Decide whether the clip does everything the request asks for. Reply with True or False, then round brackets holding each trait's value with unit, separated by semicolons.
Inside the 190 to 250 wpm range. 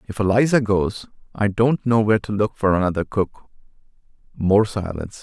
False (160 wpm)